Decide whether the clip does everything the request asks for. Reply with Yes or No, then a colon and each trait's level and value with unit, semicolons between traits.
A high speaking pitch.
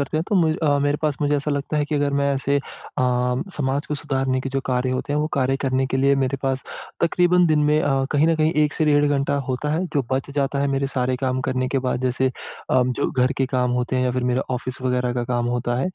No: low, 135 Hz